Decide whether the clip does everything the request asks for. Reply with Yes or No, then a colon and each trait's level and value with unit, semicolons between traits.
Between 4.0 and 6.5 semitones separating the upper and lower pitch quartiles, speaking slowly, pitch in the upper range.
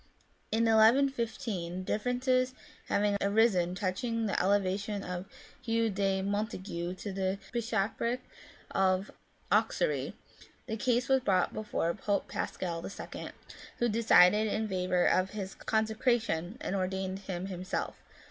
No: average, 3.4 semitones; slow, 125 wpm; high, 205 Hz